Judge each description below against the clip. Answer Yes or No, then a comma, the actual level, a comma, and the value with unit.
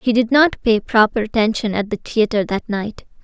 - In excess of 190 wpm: Yes, fast, 205 wpm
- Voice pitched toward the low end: No, high, 225 Hz